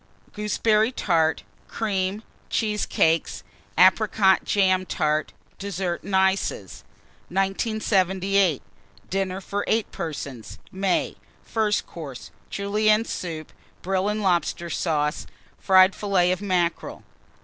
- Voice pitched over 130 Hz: Yes, high, 190 Hz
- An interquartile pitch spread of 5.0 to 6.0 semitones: No, average, 2.9 semitones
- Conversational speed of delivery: No, slow, 95 wpm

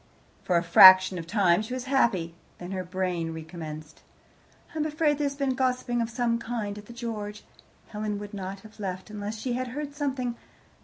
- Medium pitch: No, high, 210 Hz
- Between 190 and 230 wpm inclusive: Yes, average, 195 wpm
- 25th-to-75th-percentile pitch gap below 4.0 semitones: No, average, 5.2 semitones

